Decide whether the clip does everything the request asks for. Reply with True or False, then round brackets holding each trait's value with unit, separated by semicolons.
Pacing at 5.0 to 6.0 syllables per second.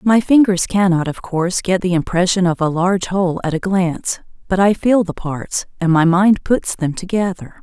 True (5.1 syllables/s)